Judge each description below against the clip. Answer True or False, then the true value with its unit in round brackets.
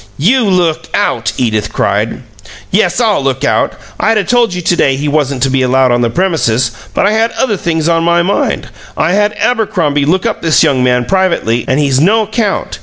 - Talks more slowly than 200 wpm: False (205 wpm)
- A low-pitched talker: False (165 Hz)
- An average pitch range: False (7.4 semitones)